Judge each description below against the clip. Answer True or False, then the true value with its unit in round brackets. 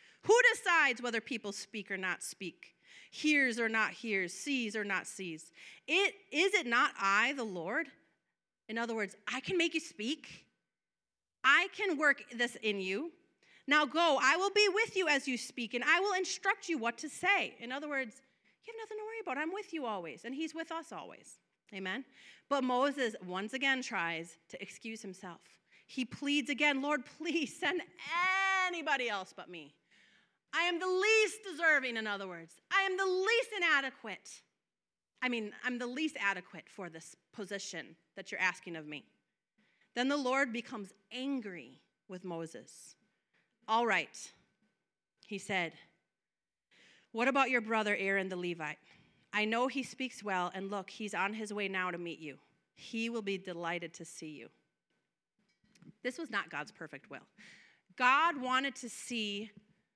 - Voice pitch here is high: True (240 Hz)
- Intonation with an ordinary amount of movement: False (7.9 semitones)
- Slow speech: False (170 wpm)